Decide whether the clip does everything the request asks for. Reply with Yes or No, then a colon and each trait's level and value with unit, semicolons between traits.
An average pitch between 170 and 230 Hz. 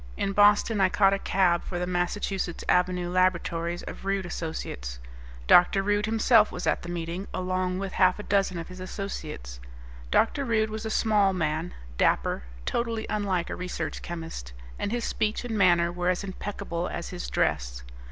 Yes: medium, 185 Hz